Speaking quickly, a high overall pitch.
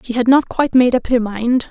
Yes: fast, 280 wpm; high, 240 Hz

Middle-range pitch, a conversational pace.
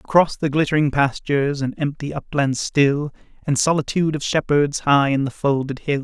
Yes: medium, 145 Hz; average, 170 wpm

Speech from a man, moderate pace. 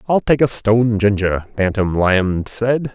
Yes: male; average, 165 wpm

